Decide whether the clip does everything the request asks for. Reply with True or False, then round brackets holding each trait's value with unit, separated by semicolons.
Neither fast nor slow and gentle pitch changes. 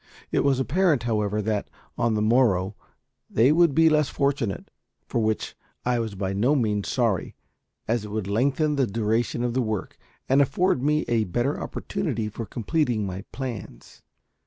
False (165 wpm; 4.6 semitones)